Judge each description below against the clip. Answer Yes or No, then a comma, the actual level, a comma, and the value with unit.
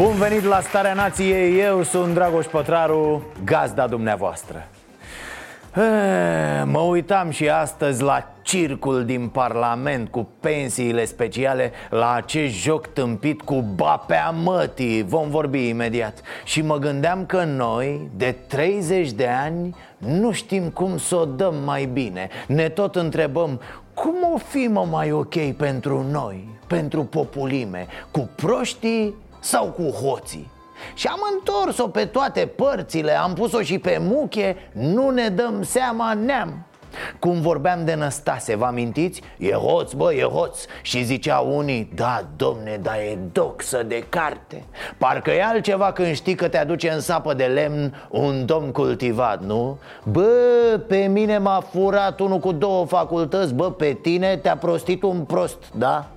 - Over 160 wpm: No, average, 145 wpm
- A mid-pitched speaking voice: Yes, medium, 165 Hz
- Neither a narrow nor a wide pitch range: No, wide, 6.1 semitones